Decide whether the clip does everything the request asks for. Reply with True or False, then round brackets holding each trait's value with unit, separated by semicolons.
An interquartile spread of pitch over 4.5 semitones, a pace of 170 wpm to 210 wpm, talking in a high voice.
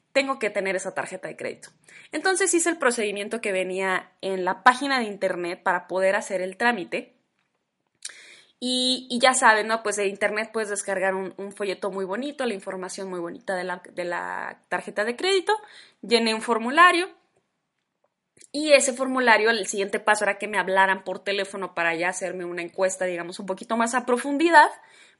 True (5.1 semitones; 180 wpm; 205 Hz)